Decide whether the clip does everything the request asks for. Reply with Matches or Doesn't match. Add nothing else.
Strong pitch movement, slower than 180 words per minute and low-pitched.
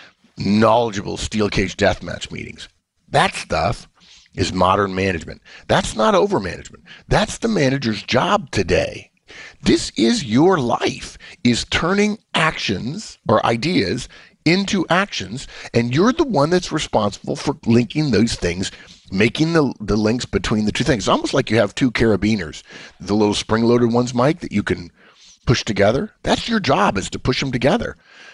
Matches